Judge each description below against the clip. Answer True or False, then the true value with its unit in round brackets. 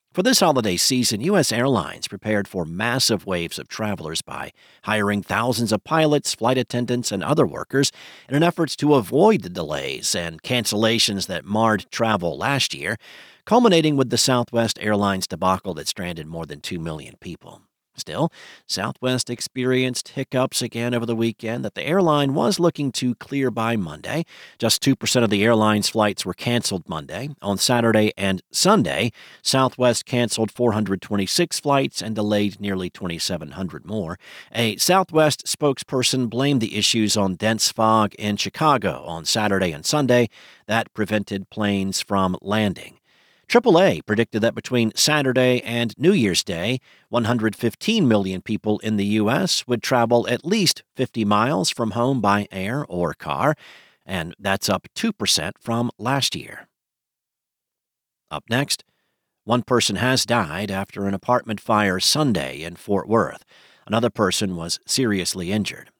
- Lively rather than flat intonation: False (4.2 semitones)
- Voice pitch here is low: True (115 Hz)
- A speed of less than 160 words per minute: True (145 wpm)